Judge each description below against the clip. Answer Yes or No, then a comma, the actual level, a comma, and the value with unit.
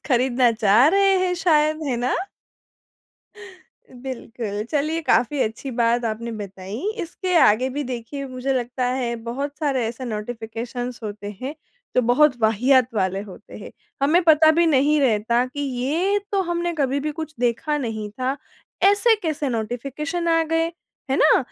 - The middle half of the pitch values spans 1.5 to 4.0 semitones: No, average, 4.6 semitones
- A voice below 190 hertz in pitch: No, very high, 255 Hz